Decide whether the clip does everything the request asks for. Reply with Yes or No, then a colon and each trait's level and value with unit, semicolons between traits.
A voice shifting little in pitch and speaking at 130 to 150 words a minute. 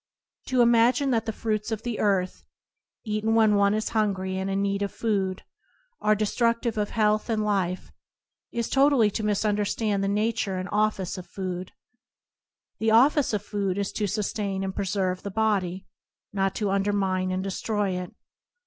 No: narrow, 2.3 semitones; average, 170 wpm